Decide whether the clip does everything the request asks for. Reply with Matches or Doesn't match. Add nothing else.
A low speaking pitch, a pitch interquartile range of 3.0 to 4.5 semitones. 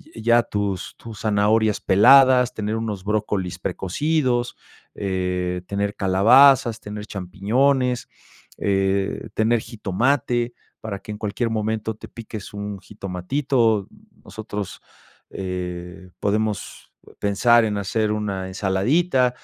Matches